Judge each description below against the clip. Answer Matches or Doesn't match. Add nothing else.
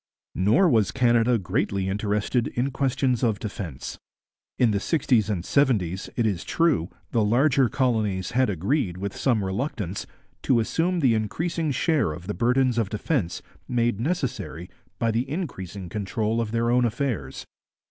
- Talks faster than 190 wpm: Doesn't match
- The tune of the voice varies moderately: Matches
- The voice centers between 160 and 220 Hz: Doesn't match